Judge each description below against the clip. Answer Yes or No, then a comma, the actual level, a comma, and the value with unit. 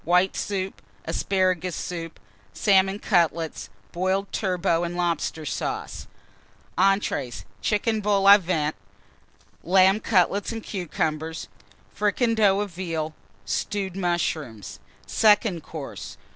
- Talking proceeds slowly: Yes, slow, 100 wpm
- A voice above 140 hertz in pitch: Yes, medium, 185 Hz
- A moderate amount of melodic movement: Yes, average, 3.2 semitones